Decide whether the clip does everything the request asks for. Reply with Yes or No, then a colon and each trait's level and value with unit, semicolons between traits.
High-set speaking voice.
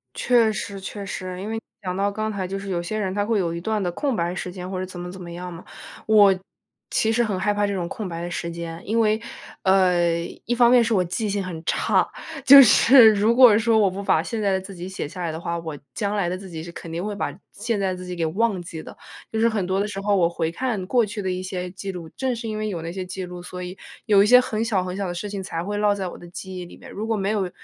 Yes: high, 195 Hz